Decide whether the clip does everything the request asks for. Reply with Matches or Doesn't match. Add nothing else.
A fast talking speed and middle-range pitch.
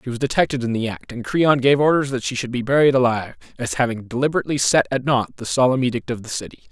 Doesn't match